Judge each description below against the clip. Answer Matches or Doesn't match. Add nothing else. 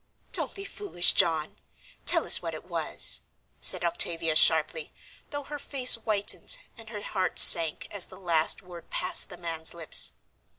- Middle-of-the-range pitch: Matches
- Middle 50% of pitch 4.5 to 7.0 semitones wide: Matches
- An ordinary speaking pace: Matches